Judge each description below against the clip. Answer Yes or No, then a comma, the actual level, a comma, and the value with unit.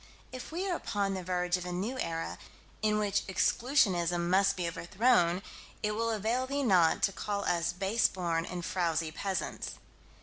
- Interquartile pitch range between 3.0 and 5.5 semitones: Yes, average, 3.7 semitones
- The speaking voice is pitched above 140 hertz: Yes, high, 190 Hz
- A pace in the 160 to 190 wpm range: Yes, average, 170 wpm